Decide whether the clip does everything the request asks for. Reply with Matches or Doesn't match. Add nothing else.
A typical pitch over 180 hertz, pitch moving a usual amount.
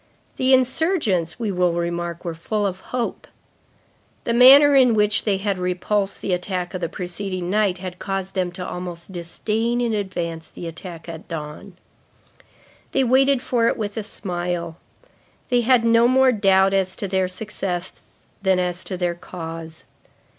Matches